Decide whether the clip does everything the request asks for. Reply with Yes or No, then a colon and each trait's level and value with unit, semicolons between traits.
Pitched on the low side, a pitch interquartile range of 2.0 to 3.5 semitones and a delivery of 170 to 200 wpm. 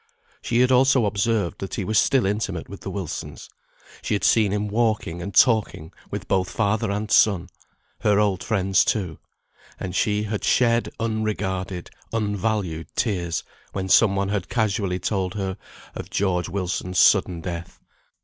No: low, 100 Hz; average, 2.8 semitones; average, 155 wpm